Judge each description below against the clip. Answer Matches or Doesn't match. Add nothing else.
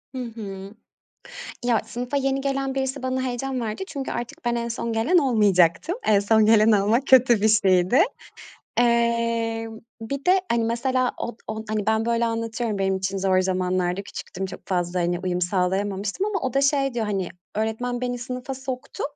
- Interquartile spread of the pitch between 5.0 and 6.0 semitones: Doesn't match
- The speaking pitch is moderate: Doesn't match